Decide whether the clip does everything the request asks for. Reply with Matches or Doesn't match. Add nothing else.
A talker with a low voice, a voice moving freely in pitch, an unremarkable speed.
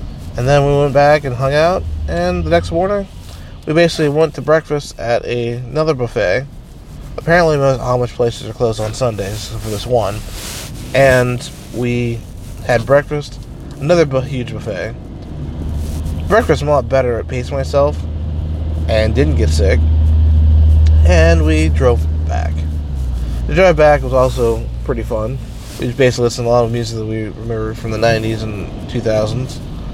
Matches